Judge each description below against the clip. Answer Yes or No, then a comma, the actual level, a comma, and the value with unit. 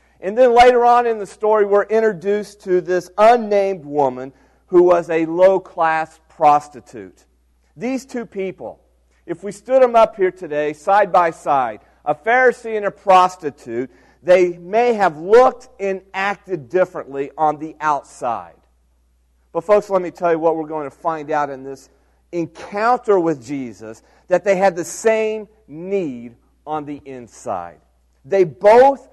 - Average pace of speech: Yes, average, 155 wpm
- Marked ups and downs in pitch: Yes, wide, 5.7 semitones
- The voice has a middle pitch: Yes, medium, 180 Hz